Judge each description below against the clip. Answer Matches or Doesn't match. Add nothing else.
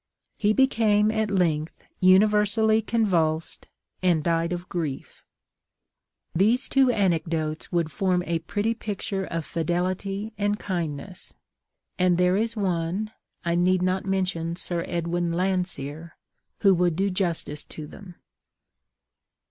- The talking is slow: Matches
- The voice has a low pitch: Doesn't match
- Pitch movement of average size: Matches